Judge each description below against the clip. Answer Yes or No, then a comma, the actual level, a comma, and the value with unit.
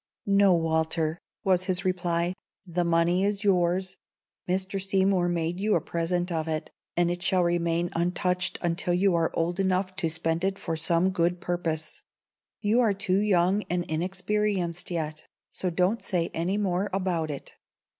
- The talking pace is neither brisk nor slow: Yes, average, 160 wpm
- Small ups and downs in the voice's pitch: Yes, narrow, 2.2 semitones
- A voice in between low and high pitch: Yes, medium, 175 Hz